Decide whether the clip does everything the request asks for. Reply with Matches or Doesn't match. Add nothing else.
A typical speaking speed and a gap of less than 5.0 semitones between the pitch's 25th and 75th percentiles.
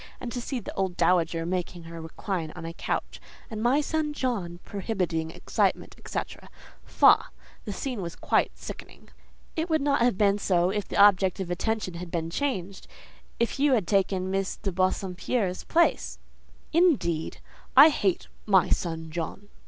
Doesn't match